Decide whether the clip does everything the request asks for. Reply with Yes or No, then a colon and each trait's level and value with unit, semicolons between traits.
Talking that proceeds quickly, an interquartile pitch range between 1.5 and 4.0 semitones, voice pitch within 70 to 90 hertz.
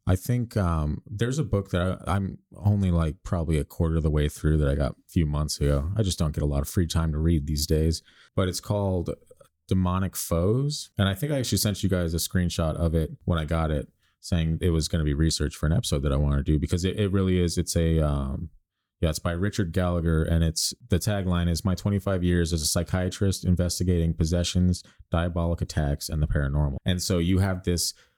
Yes: fast, 235 wpm; average, 2.9 semitones; very low, 85 Hz